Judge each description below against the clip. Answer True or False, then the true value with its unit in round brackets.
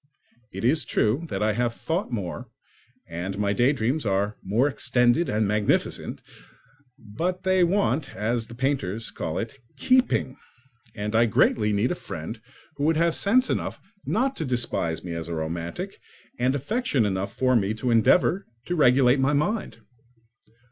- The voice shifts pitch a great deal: True (6.7 semitones)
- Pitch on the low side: True (120 Hz)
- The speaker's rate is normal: True (155 wpm)